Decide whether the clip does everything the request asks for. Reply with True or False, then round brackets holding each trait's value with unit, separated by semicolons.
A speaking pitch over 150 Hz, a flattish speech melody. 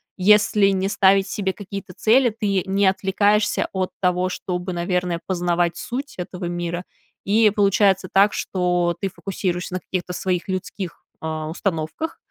True (190 Hz; 2.0 semitones)